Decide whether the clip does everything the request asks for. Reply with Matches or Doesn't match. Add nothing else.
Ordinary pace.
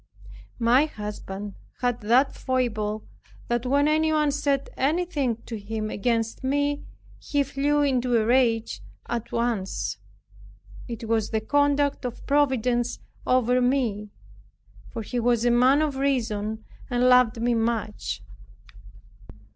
Doesn't match